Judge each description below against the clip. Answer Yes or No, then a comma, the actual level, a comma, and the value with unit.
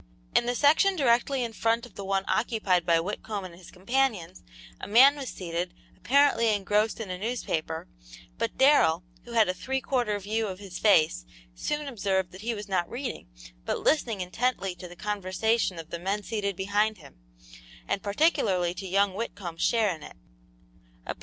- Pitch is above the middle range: Yes, high, 205 Hz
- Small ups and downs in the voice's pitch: No, average, 4.4 semitones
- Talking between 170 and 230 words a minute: Yes, average, 175 wpm